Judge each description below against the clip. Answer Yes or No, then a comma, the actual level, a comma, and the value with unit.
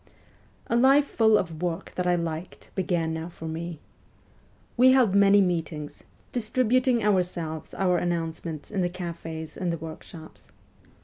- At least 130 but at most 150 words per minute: Yes, average, 140 wpm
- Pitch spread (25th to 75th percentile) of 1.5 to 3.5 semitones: No, average, 3.9 semitones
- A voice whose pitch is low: No, medium, 175 Hz